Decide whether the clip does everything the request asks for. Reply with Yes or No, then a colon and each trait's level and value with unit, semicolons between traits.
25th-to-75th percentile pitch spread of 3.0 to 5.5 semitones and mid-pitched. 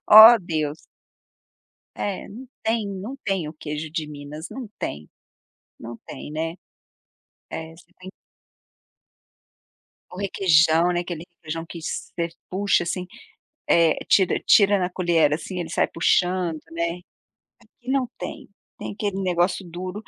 Yes: average, 3.3 semitones; medium, 175 Hz